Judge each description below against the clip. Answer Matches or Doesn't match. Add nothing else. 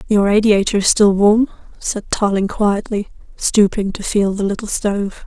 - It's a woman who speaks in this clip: Matches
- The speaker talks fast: Doesn't match